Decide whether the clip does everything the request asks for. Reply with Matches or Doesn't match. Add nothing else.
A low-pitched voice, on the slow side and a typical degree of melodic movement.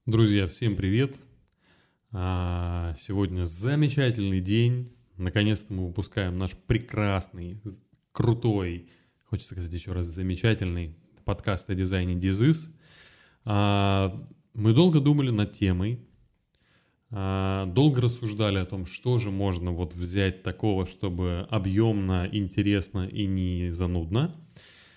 Matches